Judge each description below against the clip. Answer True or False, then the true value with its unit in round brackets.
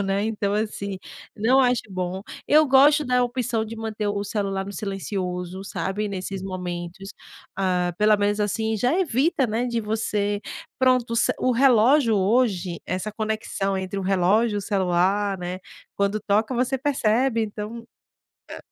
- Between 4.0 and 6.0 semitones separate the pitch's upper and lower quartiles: False (3.3 semitones)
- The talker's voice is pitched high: True (210 Hz)